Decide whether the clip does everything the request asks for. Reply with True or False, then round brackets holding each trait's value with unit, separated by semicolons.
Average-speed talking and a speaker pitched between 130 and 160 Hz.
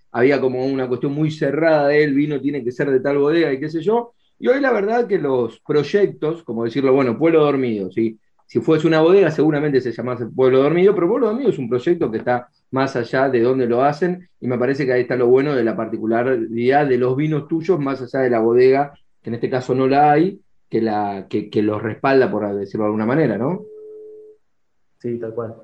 False (230 wpm; 135 Hz)